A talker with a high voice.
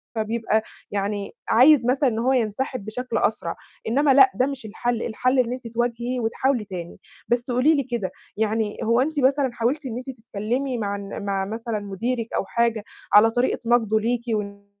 Yes: high, 235 Hz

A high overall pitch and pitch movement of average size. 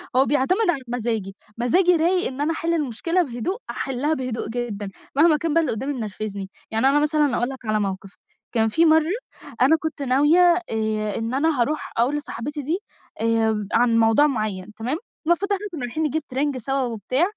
No: very high, 265 Hz; wide, 5.7 semitones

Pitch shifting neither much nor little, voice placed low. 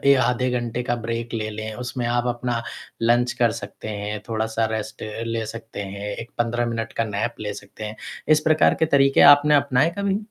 No: narrow, 2.2 semitones; low, 115 Hz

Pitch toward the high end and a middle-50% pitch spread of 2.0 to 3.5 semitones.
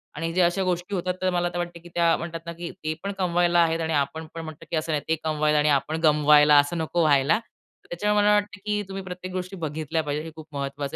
No: medium, 165 Hz; average, 2.9 semitones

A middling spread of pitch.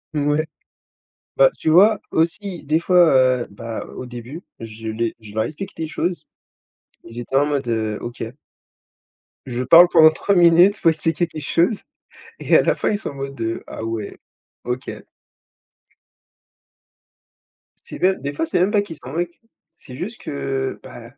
No: wide, 6.2 semitones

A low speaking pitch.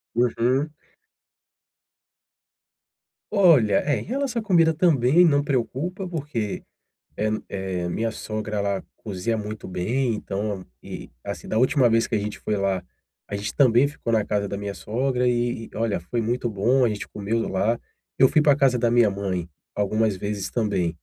Yes: low, 115 Hz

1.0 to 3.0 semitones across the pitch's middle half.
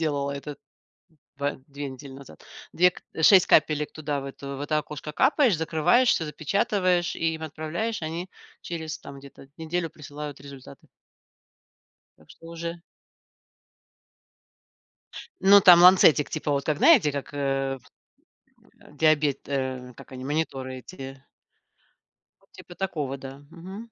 No: average, 3.4 semitones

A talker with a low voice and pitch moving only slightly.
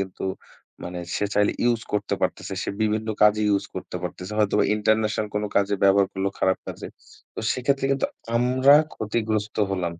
Yes: low, 105 Hz; narrow, 2.1 semitones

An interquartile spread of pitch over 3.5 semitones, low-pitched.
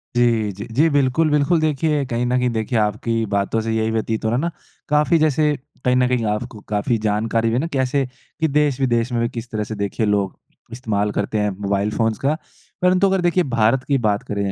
Yes: average, 4.5 semitones; low, 120 Hz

